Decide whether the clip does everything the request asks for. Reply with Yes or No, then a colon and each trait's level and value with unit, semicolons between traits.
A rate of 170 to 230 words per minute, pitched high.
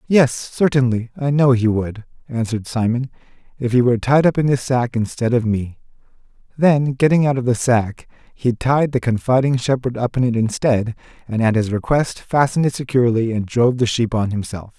No: average, 190 wpm; low, 120 Hz